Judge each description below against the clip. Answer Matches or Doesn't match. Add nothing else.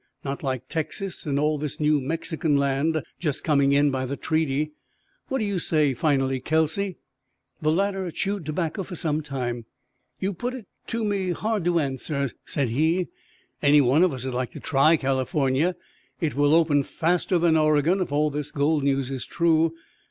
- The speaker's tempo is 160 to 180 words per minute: Matches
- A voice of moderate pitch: Matches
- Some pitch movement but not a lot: Matches